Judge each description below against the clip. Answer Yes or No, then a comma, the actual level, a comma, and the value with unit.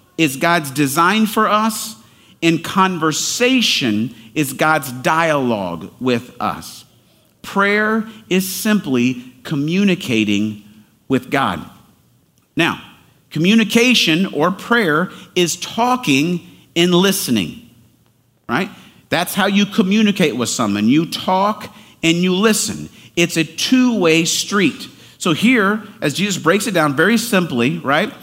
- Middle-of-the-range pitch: Yes, medium, 175 Hz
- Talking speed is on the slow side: Yes, slow, 115 wpm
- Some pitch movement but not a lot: No, wide, 5.8 semitones